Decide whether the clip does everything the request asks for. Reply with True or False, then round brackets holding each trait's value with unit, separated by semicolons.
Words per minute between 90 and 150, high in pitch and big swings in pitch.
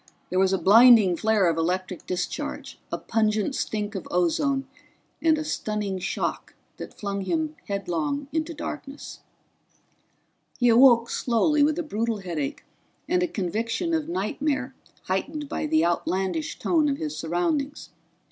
True (140 wpm; 230 Hz; 7.7 semitones)